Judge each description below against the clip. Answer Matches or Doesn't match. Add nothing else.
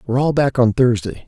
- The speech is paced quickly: Matches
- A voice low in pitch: Matches